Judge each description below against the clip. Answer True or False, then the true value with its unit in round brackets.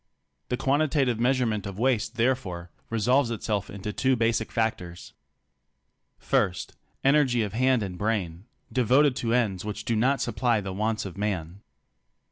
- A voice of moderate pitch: False (115 Hz)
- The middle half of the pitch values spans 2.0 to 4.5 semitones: True (3.9 semitones)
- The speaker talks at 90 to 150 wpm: True (140 wpm)